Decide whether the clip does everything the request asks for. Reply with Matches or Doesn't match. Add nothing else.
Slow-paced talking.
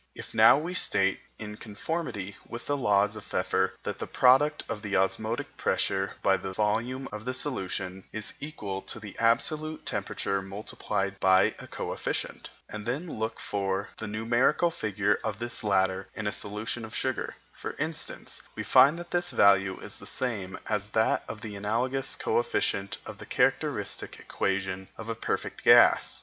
Doesn't match